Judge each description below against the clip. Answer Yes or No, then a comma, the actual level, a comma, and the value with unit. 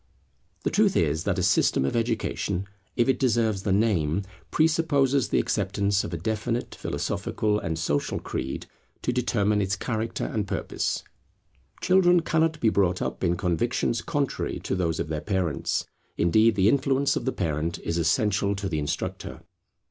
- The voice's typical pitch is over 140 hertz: No, low, 105 Hz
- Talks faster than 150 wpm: Yes, average, 160 wpm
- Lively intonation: Yes, wide, 5.7 semitones